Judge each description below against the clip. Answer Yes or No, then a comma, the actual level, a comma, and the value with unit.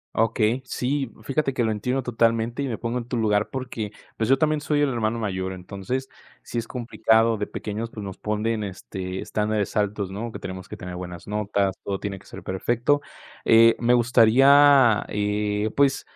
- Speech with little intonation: No, average, 3.2 semitones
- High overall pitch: No, low, 110 Hz